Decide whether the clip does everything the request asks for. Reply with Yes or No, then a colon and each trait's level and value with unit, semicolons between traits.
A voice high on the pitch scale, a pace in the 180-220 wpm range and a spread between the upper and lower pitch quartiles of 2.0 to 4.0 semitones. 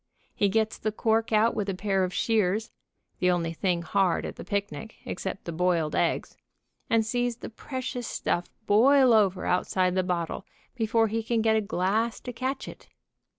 Yes: high, 215 Hz; average, 185 wpm; average, 3.7 semitones